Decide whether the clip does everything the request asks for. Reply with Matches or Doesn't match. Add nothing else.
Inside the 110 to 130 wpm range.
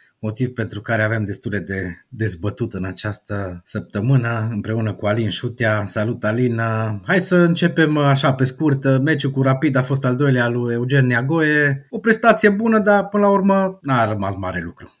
Doesn't match